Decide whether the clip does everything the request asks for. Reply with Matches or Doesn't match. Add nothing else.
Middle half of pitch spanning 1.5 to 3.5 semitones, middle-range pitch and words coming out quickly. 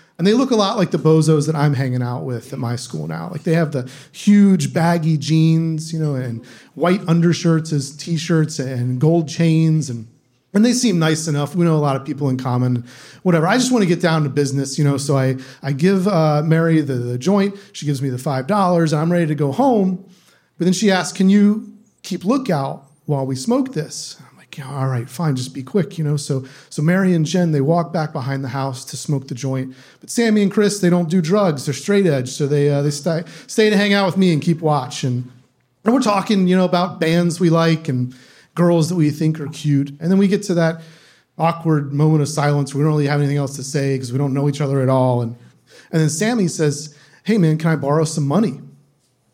Doesn't match